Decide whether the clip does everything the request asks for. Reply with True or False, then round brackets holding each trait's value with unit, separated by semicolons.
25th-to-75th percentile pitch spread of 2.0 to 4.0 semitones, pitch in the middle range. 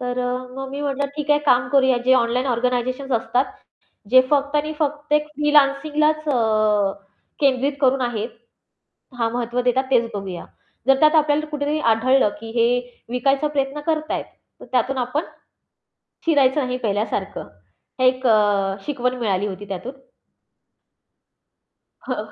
False (3.3 semitones; 255 Hz)